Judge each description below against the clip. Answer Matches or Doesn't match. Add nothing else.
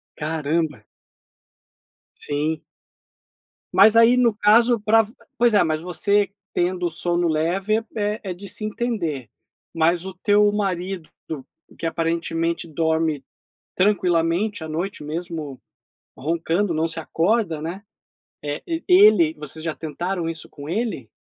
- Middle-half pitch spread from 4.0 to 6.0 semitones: Matches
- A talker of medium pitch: Matches